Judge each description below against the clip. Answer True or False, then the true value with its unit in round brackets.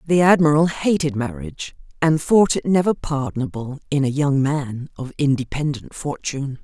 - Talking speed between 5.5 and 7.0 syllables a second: False (5.0 syllables/s)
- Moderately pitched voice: True (145 Hz)